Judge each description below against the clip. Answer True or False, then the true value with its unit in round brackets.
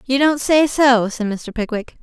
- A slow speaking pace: False (205 wpm)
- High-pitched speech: True (250 Hz)